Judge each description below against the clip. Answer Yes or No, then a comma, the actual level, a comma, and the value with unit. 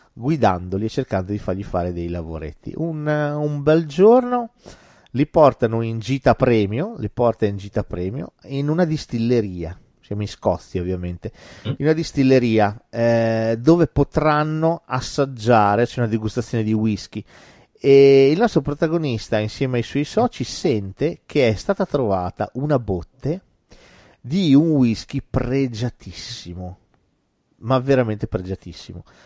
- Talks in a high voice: No, low, 120 Hz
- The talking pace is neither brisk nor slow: Yes, average, 130 wpm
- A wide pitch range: Yes, wide, 5.7 semitones